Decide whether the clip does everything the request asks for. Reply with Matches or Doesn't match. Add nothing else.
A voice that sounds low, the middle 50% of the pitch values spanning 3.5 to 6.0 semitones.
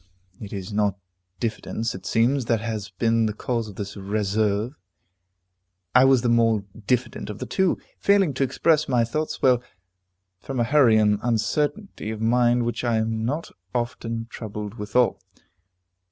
Doesn't match